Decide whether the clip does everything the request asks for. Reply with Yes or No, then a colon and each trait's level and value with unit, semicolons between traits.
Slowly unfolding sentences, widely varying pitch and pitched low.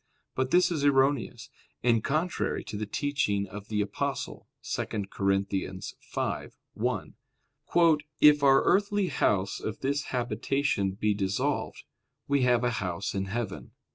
Yes: slow, 130 wpm; wide, 6.1 semitones; low, 115 Hz